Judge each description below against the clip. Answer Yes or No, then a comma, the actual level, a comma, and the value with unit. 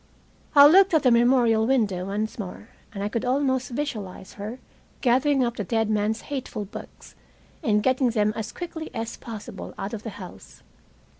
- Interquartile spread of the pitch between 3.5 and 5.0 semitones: Yes, average, 3.8 semitones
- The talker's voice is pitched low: No, high, 230 Hz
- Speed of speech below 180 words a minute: Yes, average, 170 wpm